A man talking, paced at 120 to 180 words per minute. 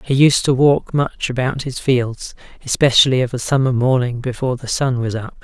No: male; average, 200 wpm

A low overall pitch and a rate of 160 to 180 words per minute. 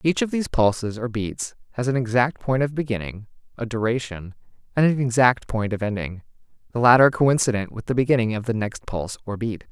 No: low, 120 Hz; average, 200 wpm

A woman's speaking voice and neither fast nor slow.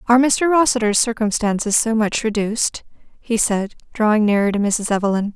Yes: female; average, 155 wpm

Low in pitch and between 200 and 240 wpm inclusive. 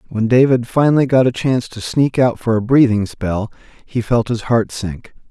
Yes: low, 120 Hz; fast, 205 wpm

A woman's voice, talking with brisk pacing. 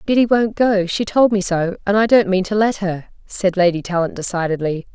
Yes: female; fast, 220 wpm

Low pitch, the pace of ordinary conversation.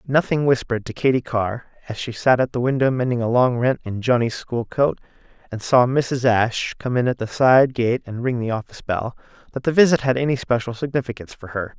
No: low, 125 Hz; fast, 220 wpm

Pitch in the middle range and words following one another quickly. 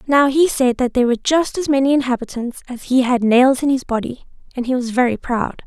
No: very high, 255 Hz; fast, 235 wpm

